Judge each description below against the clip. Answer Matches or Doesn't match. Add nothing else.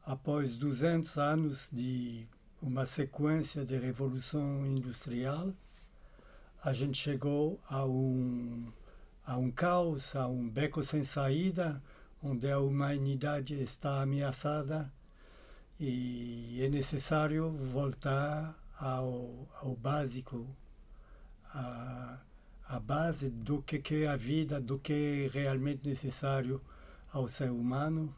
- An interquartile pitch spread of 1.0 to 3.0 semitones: Matches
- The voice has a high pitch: Doesn't match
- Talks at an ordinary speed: Doesn't match